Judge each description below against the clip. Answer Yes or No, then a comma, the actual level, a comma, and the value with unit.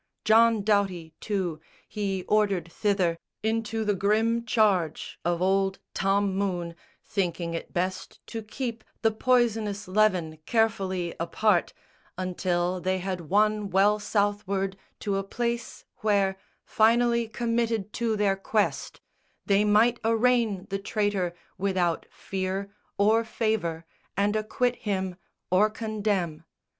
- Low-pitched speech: No, high, 200 Hz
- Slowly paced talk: Yes, slow, 120 wpm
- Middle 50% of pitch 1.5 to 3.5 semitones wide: Yes, average, 2.8 semitones